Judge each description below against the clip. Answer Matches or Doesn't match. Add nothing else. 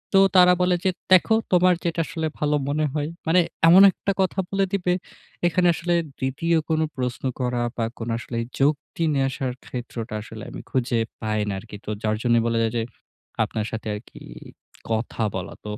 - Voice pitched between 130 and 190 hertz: Matches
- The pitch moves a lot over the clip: Matches